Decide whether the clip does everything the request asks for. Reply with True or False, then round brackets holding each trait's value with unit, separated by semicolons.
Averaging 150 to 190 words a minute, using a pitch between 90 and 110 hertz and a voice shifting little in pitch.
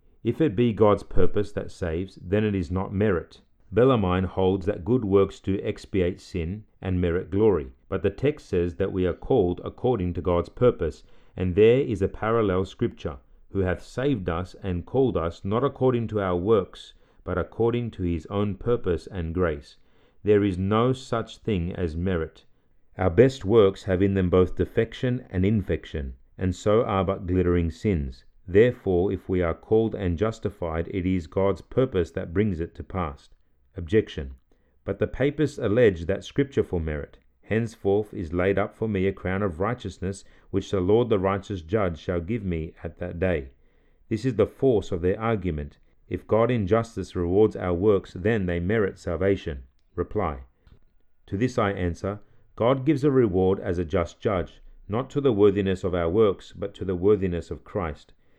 False (180 wpm; 95 Hz; 3.5 semitones)